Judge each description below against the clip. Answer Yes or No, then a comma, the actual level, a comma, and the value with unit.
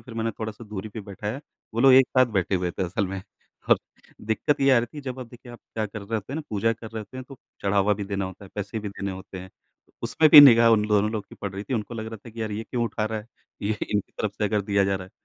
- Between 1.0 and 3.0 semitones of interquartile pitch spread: Yes, narrow, 2.6 semitones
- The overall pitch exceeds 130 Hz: No, low, 110 Hz